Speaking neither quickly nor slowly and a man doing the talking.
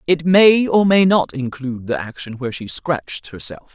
No: average, 190 wpm; female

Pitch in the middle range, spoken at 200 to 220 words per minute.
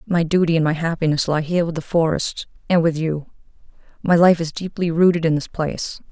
Yes: medium, 165 Hz; fast, 205 wpm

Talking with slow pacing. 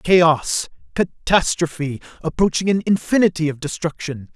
Yes: slow, 95 wpm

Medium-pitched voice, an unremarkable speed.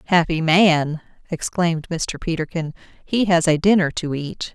Yes: medium, 165 Hz; average, 145 wpm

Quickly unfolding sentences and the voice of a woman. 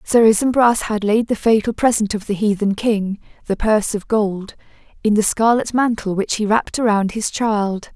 No: average, 190 wpm; female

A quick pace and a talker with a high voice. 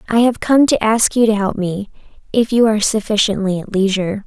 Yes: fast, 210 wpm; high, 215 Hz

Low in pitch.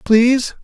No: high, 240 Hz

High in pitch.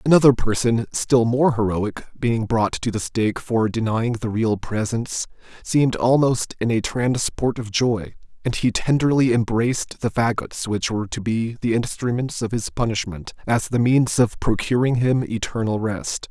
No: low, 115 Hz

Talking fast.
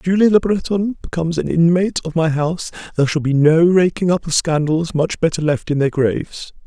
Yes: fast, 215 wpm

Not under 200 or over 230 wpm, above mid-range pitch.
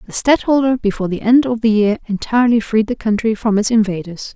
Yes: fast, 205 wpm; high, 220 Hz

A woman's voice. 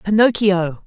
Yes: female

